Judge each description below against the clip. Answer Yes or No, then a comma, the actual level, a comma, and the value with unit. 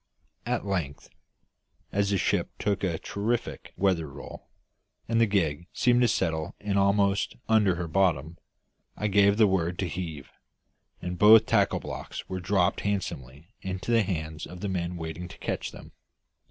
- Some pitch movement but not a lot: Yes, average, 3.4 semitones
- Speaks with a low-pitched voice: Yes, very low, 95 Hz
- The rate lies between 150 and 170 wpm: Yes, average, 160 wpm